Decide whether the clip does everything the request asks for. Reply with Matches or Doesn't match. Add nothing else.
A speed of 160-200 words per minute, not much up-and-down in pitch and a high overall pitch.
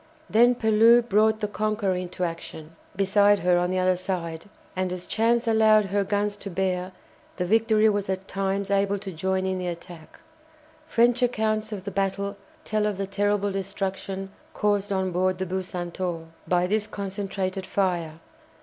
Matches